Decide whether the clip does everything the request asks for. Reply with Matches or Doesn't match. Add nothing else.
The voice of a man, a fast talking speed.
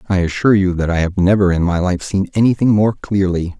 Matches